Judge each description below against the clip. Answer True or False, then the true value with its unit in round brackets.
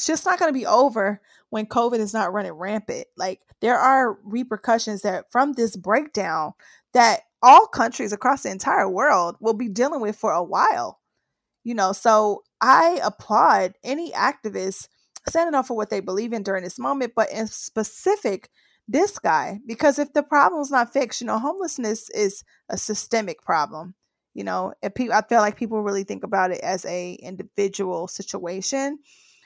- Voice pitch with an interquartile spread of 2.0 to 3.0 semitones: False (5.0 semitones)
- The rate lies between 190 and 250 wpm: False (175 wpm)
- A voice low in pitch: False (220 Hz)